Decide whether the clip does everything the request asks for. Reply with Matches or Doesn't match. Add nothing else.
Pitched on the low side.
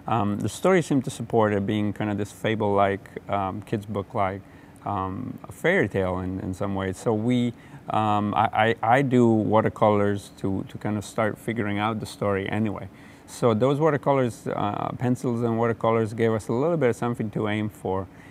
Matches